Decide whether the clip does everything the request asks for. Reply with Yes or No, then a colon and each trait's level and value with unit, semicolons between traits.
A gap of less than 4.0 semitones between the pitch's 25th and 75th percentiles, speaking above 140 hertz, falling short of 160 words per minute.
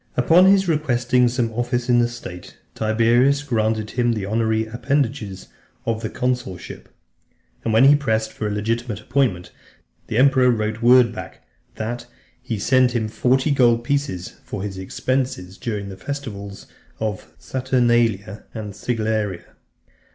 No: average, 2.8 semitones; low, 115 Hz; average, 145 wpm